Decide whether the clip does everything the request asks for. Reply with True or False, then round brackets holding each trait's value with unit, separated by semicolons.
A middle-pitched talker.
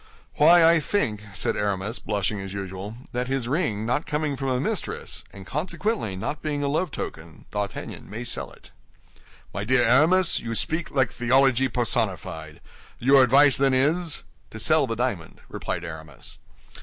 False (125 Hz)